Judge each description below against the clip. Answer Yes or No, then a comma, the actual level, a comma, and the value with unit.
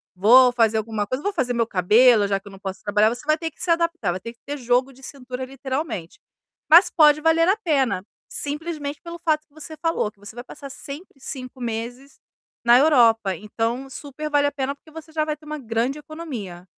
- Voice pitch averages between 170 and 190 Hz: No, very high, 265 Hz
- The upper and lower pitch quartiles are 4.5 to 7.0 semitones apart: Yes, average, 5.2 semitones